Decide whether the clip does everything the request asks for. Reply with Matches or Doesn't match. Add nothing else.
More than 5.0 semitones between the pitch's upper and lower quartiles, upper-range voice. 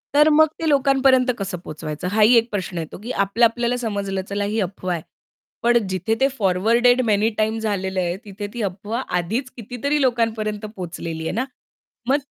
Doesn't match